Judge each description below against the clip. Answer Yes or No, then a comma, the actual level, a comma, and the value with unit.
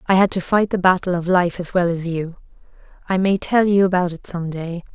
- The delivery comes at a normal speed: No, fast, 245 wpm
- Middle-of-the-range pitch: Yes, medium, 180 Hz